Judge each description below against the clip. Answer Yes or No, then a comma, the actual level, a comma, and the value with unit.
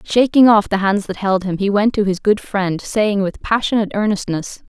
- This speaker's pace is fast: Yes, fast, 215 wpm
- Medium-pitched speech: No, high, 205 Hz